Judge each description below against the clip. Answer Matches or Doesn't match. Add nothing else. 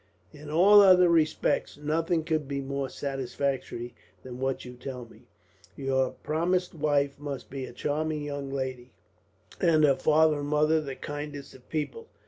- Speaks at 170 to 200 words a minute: Doesn't match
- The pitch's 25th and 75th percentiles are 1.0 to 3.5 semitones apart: Matches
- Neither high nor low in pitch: Matches